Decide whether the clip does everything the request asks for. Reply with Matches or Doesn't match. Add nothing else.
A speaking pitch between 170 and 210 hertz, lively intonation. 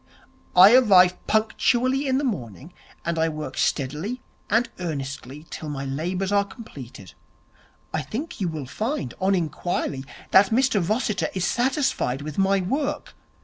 Matches